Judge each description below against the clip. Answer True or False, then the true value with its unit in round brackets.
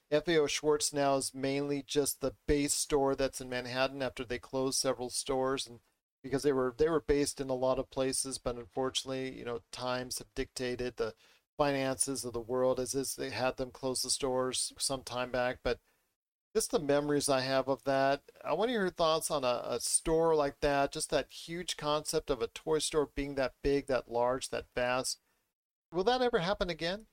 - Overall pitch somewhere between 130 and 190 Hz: True (135 Hz)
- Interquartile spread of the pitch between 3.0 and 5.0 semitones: False (2.6 semitones)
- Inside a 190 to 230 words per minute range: True (200 wpm)